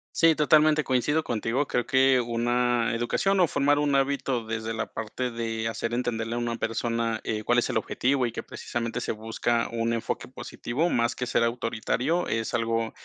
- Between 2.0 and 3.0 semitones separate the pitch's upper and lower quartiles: Yes, average, 2.7 semitones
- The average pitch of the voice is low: Yes, low, 120 Hz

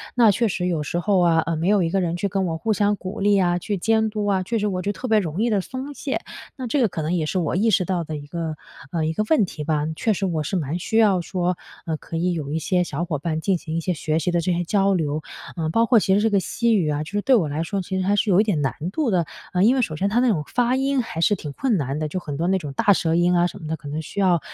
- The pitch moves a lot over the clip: No, average, 4.2 semitones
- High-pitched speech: No, medium, 180 Hz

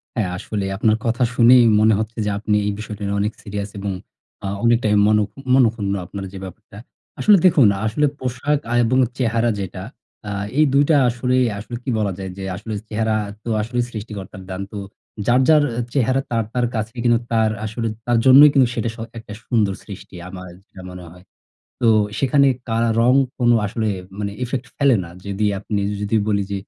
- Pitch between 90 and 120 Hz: Yes, low, 110 Hz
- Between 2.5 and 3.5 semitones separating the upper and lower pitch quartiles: Yes, average, 3.2 semitones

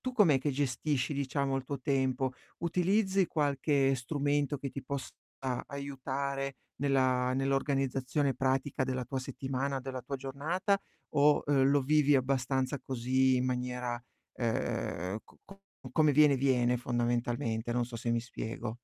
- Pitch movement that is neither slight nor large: No, narrow, 2.1 semitones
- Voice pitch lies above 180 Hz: No, low, 135 Hz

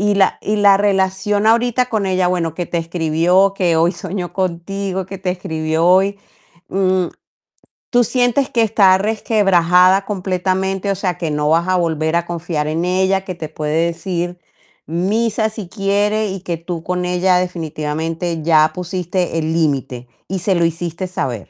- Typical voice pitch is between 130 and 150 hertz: No, medium, 180 Hz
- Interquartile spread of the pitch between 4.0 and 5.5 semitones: No, average, 2.8 semitones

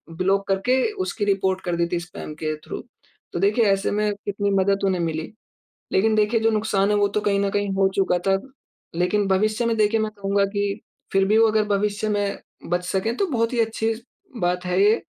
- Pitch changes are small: Yes, narrow, 2.0 semitones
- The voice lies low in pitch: No, high, 200 Hz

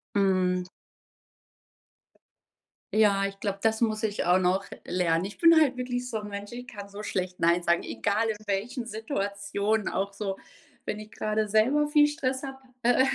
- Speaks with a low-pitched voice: No, high, 210 Hz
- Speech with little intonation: No, average, 3.7 semitones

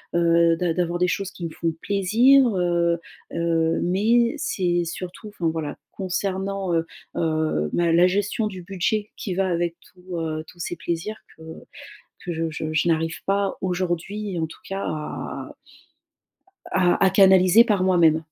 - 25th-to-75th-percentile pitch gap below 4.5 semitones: Yes, average, 2.8 semitones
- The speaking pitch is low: No, medium, 180 Hz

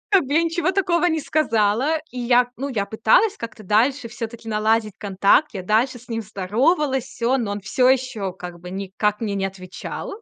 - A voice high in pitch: Yes, high, 230 Hz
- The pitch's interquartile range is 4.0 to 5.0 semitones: Yes, average, 4.7 semitones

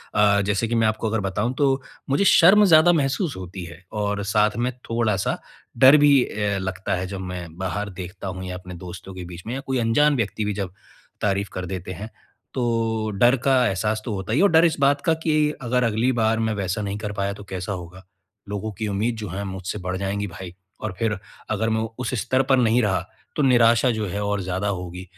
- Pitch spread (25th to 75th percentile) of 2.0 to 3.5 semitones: No, average, 4.0 semitones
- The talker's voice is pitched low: Yes, low, 105 Hz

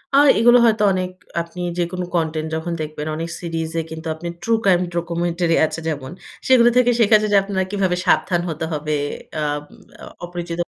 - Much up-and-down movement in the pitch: No, average, 3.0 semitones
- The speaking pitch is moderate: Yes, medium, 170 Hz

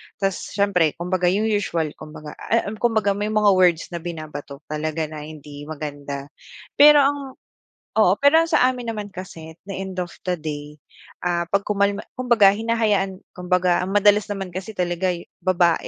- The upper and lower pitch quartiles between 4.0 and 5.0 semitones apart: Yes, average, 4.3 semitones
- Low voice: No, medium, 185 Hz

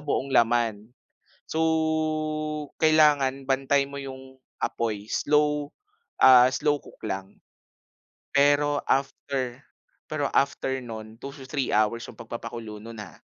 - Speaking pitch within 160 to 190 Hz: No, low, 130 Hz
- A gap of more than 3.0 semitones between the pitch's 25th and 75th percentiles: Yes, average, 3.5 semitones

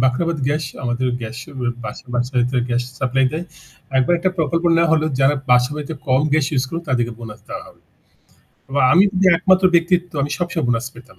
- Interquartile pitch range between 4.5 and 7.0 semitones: Yes, average, 5.1 semitones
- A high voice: No, medium, 140 Hz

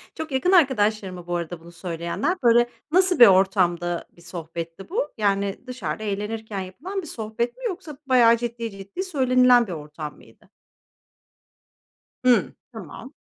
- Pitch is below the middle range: No, high, 215 Hz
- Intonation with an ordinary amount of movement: No, wide, 6.4 semitones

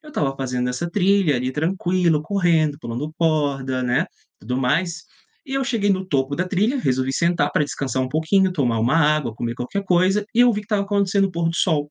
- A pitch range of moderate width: No, wide, 6.4 semitones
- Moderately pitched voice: Yes, medium, 165 Hz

